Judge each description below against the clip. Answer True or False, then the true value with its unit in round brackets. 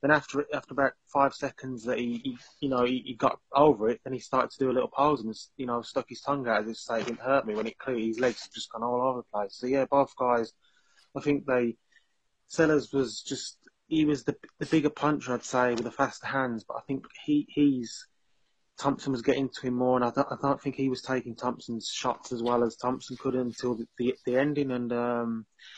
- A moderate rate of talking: False (245 wpm)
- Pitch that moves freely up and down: False (2.5 semitones)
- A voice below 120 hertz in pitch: False (130 Hz)